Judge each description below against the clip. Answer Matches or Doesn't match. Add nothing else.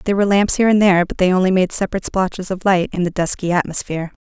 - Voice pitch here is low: Doesn't match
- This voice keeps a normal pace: Doesn't match